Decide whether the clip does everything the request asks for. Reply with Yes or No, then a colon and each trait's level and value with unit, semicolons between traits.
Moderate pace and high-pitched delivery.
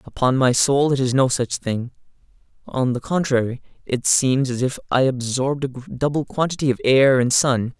No: average, 185 wpm; low, 130 Hz